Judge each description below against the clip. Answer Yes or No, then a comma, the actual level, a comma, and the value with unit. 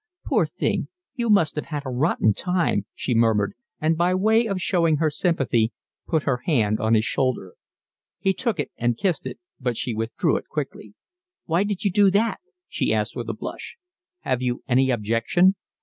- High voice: No, medium, 150 Hz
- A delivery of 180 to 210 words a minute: Yes, average, 185 wpm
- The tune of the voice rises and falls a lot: Yes, wide, 7.5 semitones